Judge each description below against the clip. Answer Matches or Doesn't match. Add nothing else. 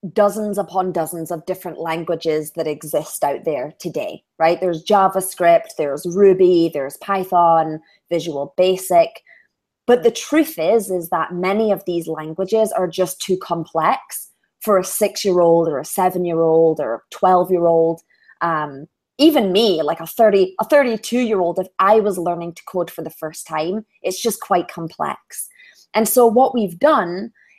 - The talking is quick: Doesn't match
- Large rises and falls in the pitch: Doesn't match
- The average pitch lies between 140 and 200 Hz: Matches